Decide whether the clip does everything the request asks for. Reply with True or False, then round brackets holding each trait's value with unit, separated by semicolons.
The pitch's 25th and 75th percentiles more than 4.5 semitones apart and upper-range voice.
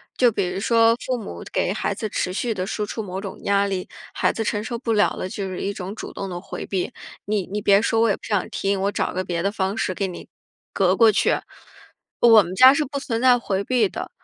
False (3.0 semitones; 205 Hz)